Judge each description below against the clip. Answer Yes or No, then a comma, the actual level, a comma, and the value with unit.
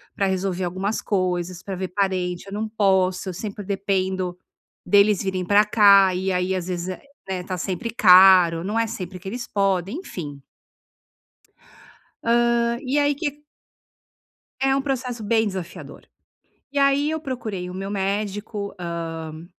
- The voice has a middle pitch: No, high, 195 Hz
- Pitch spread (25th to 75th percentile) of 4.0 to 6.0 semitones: No, average, 3.2 semitones